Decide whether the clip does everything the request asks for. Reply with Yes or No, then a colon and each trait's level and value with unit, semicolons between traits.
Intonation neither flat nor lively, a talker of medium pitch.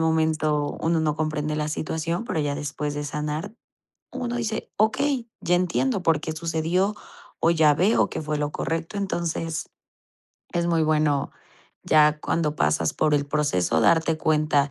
No: narrow, 2.1 semitones; medium, 155 Hz